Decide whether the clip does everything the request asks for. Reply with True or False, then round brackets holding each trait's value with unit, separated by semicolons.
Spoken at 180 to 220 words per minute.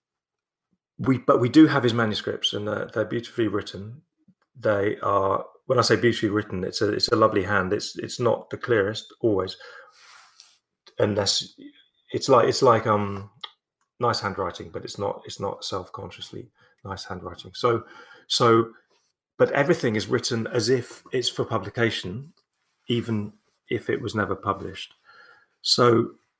False (150 wpm)